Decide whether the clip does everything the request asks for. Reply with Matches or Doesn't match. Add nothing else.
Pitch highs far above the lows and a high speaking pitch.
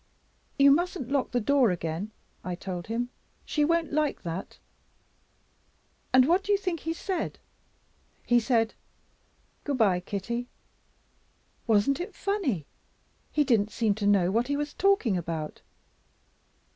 Matches